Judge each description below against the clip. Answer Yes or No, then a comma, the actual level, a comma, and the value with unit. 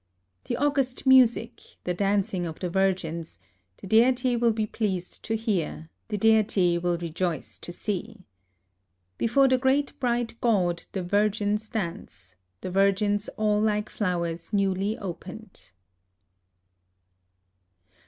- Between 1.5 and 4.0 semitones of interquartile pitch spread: No, average, 4.4 semitones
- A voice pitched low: No, high, 200 Hz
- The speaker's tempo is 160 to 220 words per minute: No, slow, 135 wpm